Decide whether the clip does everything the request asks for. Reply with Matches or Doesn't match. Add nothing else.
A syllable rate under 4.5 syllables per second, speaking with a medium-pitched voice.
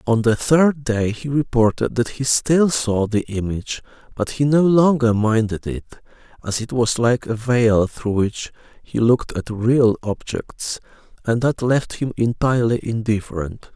Doesn't match